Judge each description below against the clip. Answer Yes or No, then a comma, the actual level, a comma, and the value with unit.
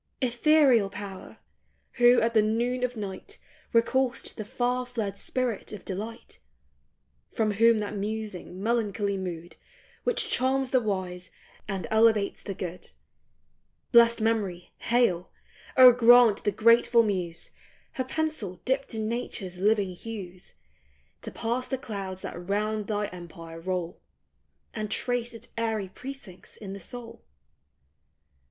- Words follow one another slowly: Yes, slow, 130 wpm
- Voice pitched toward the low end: No, high, 220 Hz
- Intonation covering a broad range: No, average, 3.8 semitones